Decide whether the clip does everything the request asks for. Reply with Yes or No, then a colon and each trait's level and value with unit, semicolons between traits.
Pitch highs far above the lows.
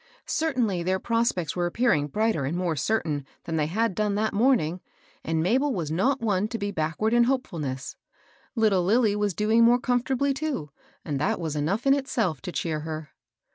Yes: wide, 6.5 semitones